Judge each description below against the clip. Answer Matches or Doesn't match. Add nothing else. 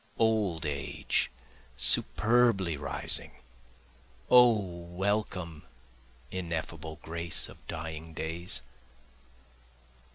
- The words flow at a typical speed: Doesn't match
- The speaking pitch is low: Matches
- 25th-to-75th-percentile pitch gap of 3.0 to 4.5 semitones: Matches